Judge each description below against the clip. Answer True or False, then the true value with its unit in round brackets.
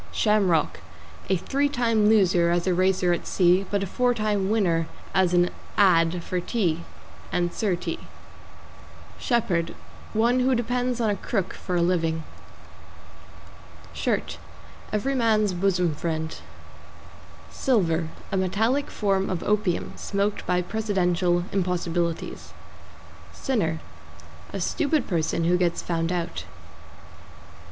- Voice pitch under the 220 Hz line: True (185 Hz)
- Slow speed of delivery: True (120 wpm)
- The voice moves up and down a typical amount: True (3.8 semitones)